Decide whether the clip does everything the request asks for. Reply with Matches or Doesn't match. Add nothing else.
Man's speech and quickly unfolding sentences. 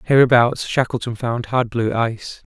Doesn't match